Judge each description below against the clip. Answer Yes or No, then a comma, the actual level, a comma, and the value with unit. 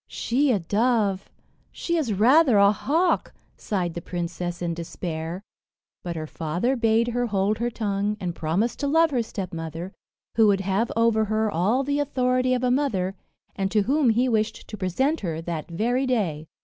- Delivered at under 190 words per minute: Yes, average, 175 wpm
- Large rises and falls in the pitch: Yes, wide, 5.7 semitones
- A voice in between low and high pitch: No, high, 215 Hz